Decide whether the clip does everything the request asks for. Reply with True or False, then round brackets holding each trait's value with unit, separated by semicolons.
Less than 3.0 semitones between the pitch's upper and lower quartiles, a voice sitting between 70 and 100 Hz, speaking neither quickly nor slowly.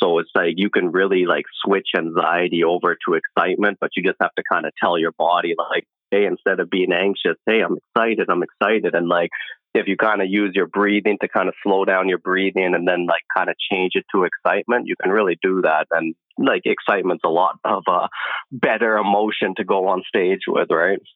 False (2.4 semitones; 95 Hz; 220 wpm)